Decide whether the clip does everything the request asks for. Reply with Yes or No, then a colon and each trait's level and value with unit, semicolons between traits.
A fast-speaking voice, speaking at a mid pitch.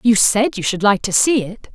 No: fast, 275 wpm; high, 210 Hz